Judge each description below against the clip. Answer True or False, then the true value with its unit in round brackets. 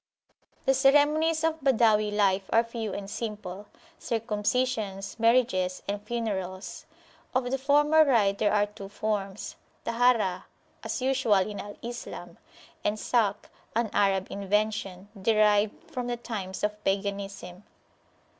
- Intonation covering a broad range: False (3.5 semitones)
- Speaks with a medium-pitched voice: False (210 Hz)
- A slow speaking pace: True (120 wpm)